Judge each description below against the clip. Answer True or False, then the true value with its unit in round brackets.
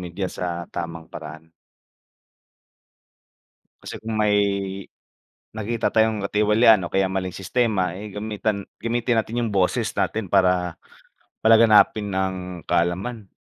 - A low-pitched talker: True (100 Hz)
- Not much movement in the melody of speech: False (3.4 semitones)